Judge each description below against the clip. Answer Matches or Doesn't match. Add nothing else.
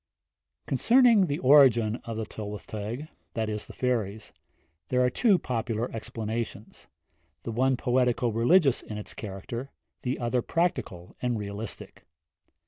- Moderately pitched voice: Doesn't match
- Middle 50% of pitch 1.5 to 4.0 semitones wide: Matches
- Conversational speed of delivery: Doesn't match